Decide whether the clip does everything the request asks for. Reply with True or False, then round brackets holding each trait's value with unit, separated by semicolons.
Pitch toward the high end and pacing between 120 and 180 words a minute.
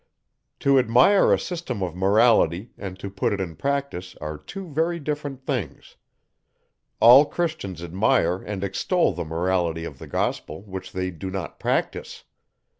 False (100 Hz; 150 wpm)